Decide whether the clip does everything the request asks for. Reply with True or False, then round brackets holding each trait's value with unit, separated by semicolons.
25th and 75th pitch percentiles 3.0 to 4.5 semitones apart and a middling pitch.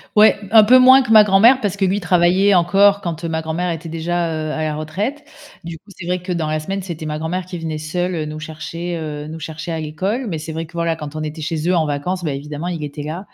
True (3.3 semitones; 170 Hz)